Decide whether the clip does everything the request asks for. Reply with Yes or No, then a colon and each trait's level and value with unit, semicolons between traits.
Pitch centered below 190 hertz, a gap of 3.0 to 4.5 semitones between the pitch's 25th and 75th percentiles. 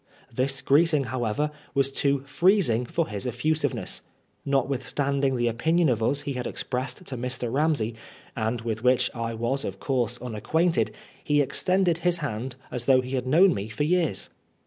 Yes: low, 135 Hz; average, 3.9 semitones